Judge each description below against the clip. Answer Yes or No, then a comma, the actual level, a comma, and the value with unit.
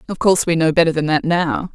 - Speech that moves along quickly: Yes, fast, 275 wpm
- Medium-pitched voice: Yes, medium, 165 Hz